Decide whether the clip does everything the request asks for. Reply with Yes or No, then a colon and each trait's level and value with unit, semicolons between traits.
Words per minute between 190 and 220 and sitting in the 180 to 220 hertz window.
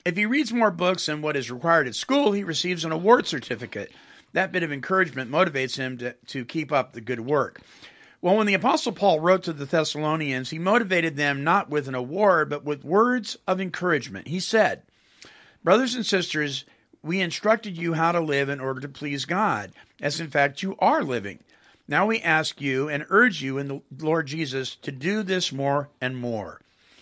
No: average, 200 wpm; medium, 160 Hz